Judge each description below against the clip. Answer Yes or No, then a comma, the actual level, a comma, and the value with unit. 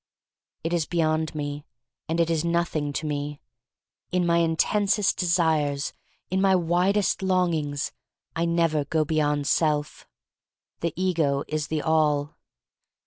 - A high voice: No, medium, 160 Hz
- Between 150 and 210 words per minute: No, average, 140 wpm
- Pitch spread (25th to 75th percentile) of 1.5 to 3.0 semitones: Yes, narrow, 2.5 semitones